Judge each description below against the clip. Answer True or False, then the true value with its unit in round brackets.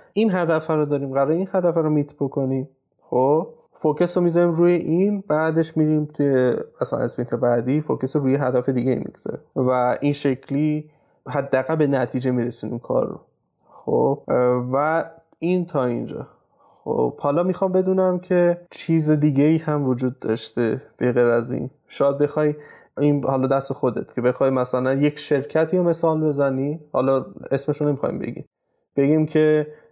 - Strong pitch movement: False (3.4 semitones)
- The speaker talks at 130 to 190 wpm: True (155 wpm)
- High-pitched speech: False (145 Hz)